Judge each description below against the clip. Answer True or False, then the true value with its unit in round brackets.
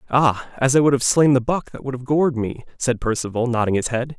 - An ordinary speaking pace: False (260 wpm)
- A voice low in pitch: True (130 Hz)